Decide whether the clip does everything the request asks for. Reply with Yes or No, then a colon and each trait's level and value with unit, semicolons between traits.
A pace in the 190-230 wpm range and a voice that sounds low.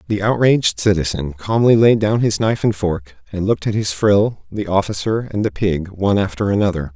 Yes: average, 200 wpm; low, 100 Hz